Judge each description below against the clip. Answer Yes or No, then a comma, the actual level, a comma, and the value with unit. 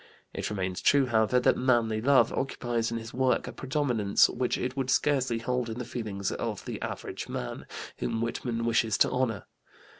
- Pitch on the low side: Yes, low, 120 Hz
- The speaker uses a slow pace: No, average, 180 wpm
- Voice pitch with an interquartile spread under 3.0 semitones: Yes, narrow, 2.4 semitones